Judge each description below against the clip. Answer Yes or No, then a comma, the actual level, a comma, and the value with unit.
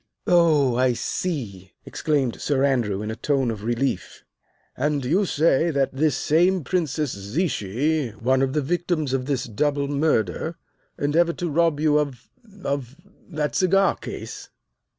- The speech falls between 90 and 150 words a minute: Yes, average, 145 wpm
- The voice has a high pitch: No, medium, 140 Hz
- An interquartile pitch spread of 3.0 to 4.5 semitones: Yes, average, 4.0 semitones